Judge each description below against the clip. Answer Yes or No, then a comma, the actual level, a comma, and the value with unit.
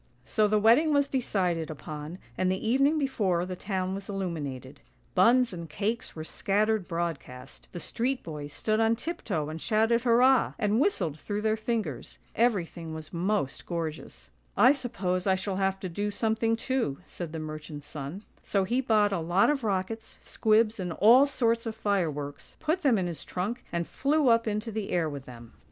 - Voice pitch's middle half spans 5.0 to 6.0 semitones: Yes, wide, 5.6 semitones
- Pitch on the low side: No, high, 200 Hz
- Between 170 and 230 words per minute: Yes, average, 185 wpm